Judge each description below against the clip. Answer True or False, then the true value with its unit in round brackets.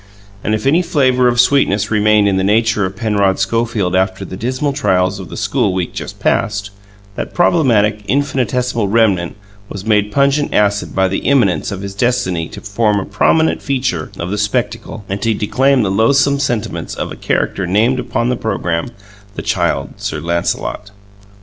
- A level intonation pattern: False (4.4 semitones)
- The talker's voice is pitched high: False (105 Hz)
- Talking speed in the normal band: True (175 wpm)